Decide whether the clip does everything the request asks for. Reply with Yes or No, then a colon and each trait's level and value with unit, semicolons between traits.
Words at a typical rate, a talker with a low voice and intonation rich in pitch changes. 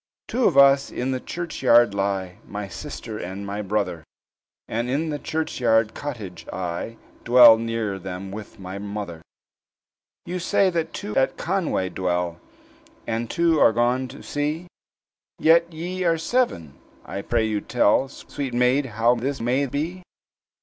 Yes: average, 150 wpm; low, 120 Hz; wide, 6.5 semitones